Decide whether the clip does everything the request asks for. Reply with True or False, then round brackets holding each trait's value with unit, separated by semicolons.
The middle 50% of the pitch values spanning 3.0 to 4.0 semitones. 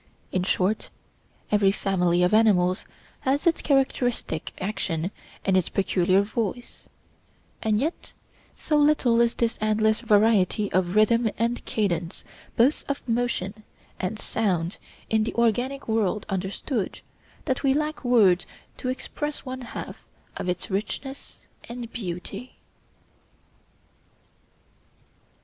False (4.4 semitones)